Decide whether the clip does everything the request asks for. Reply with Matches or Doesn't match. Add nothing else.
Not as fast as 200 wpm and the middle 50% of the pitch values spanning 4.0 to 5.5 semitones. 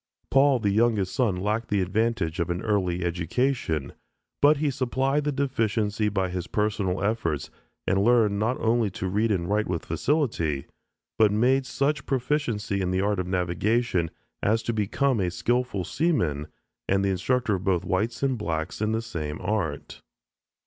Matches